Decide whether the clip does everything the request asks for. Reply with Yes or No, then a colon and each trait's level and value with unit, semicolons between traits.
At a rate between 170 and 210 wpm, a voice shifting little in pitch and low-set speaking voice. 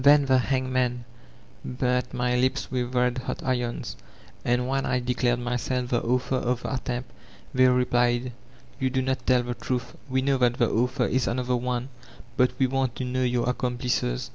Yes: average, 180 wpm; narrow, 0.9 semitones; low, 125 Hz